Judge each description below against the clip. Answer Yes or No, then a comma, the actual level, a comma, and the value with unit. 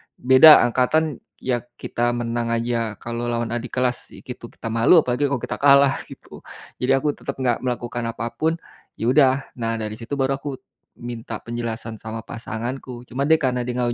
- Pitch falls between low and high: No, low, 120 Hz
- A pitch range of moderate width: No, narrow, 2.2 semitones